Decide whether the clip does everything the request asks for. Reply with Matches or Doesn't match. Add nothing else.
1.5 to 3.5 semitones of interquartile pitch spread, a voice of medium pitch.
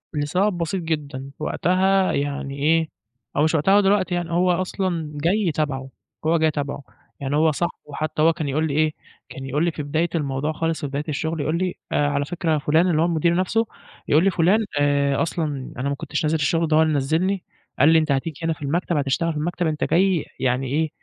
Matches